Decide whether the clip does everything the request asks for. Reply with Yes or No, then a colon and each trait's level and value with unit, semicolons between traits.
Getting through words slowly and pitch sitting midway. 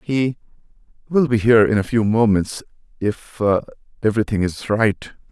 No: slow, 115 wpm; low, 110 Hz